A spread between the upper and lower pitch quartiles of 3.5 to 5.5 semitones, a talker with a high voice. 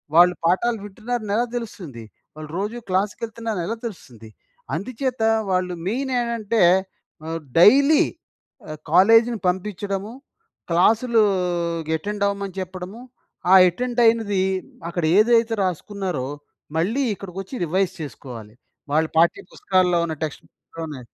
Yes: average, 4.7 semitones; high, 195 Hz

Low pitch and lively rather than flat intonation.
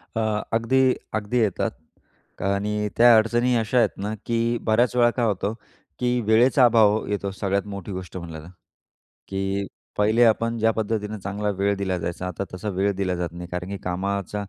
No: low, 105 Hz; average, 2.8 semitones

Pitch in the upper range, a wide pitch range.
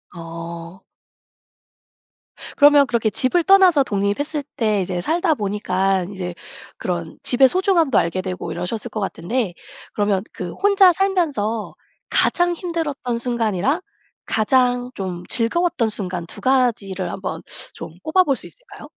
Yes: high, 225 Hz; wide, 7.9 semitones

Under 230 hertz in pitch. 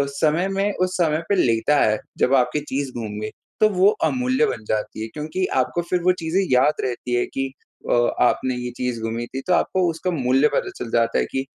Yes: medium, 140 Hz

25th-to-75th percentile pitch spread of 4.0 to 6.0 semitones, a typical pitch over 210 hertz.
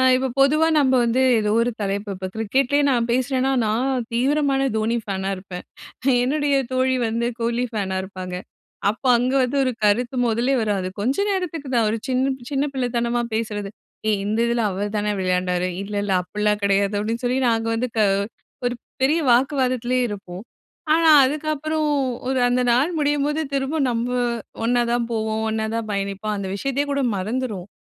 Yes: average, 4.3 semitones; high, 235 Hz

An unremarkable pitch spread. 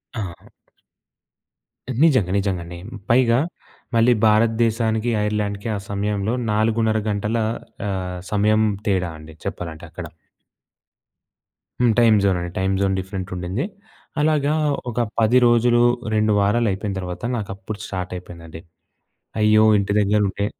Yes: average, 3.1 semitones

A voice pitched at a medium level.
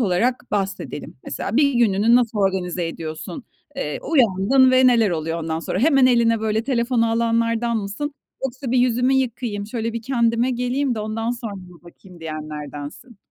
No: high, 230 Hz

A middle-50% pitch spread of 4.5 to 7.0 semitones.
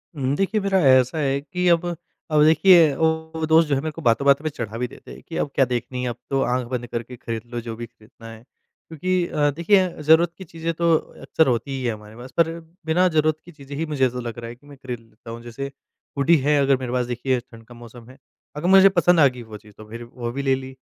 Yes: average, 5.0 semitones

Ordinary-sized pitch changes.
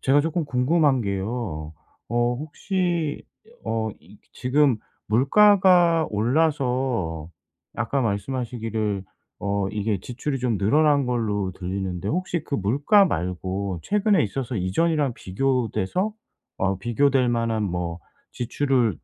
No: wide, 6.5 semitones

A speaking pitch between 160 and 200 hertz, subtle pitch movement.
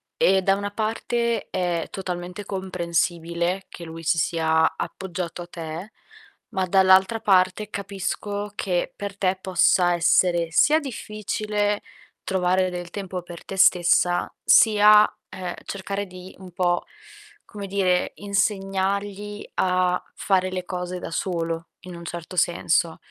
Yes: medium, 185 Hz; narrow, 2.3 semitones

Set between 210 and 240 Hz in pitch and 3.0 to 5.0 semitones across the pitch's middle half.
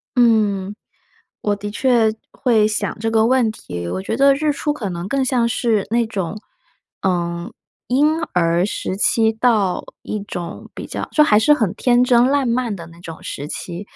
Yes: high, 220 Hz; average, 4.6 semitones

